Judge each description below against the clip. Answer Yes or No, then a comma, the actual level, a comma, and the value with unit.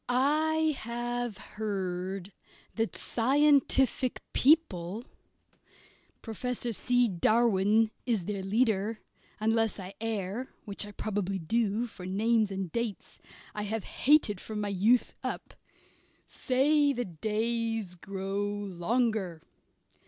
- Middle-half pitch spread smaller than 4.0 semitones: Yes, average, 3.6 semitones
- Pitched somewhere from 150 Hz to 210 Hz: No, high, 220 Hz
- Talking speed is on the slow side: Yes, slow, 105 wpm